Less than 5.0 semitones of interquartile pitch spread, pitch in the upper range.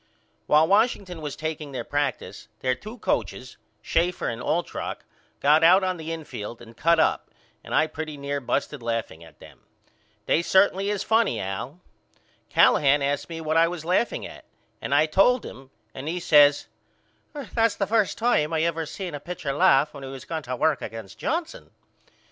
No: average, 4.4 semitones; medium, 155 Hz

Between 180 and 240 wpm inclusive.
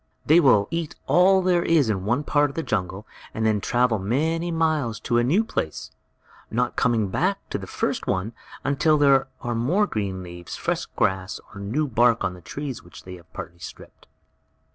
Yes: average, 190 wpm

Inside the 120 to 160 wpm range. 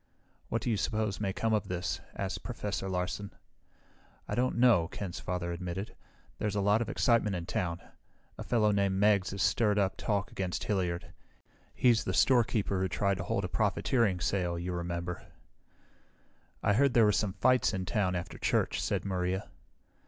No: average, 175 wpm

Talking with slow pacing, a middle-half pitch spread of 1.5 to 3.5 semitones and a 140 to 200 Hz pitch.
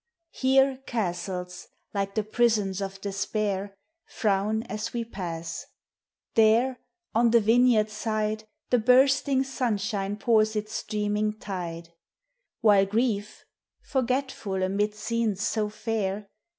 No: slow, 110 wpm; average, 2.8 semitones; high, 215 Hz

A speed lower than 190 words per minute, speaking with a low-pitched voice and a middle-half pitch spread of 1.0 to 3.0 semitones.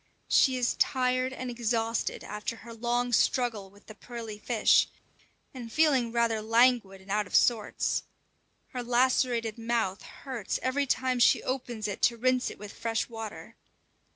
No: average, 155 wpm; high, 235 Hz; narrow, 2.4 semitones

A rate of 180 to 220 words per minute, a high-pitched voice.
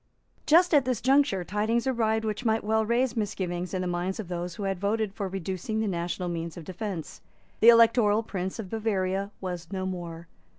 Yes: average, 195 wpm; high, 200 Hz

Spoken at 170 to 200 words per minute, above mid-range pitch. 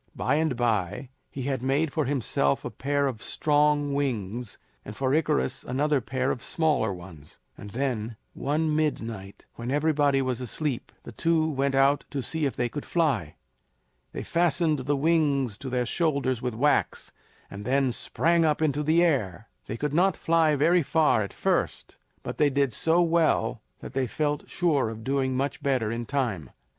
No: average, 175 wpm; medium, 140 Hz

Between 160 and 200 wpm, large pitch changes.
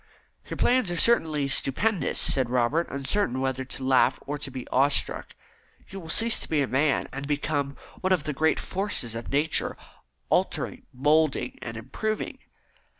No: average, 165 wpm; average, 3.8 semitones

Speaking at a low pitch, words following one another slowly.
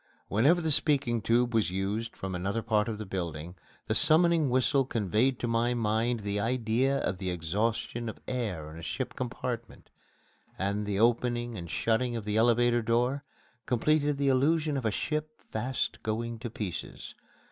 No: low, 115 Hz; average, 170 wpm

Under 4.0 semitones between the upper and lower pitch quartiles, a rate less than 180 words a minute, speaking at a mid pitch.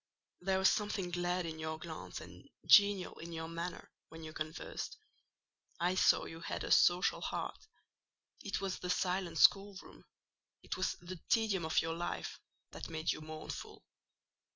Yes: average, 2.7 semitones; average, 150 wpm; medium, 175 Hz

